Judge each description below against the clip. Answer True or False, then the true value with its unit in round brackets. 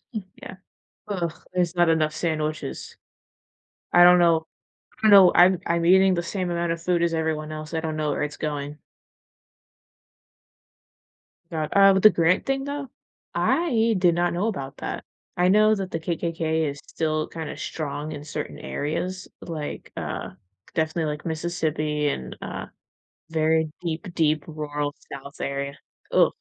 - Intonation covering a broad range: False (2.7 semitones)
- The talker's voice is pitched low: False (165 Hz)